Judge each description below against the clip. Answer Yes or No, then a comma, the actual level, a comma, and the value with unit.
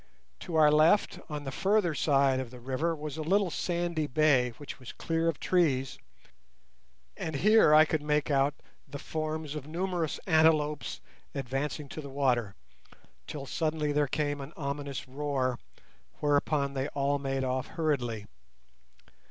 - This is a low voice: No, medium, 150 Hz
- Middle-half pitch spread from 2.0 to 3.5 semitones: Yes, narrow, 2.6 semitones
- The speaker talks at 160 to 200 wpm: No, average, 150 wpm